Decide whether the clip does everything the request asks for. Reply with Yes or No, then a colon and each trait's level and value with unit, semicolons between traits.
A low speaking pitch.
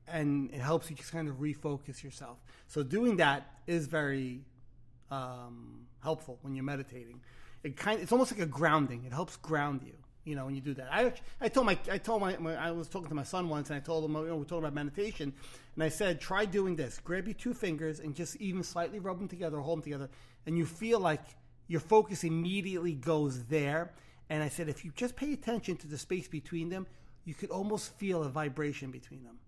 No: medium, 155 Hz